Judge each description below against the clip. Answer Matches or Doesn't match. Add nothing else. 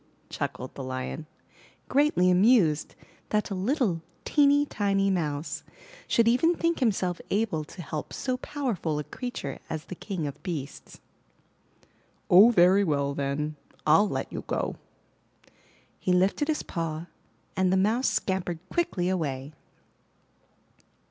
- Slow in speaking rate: Matches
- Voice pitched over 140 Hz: Matches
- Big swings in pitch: Matches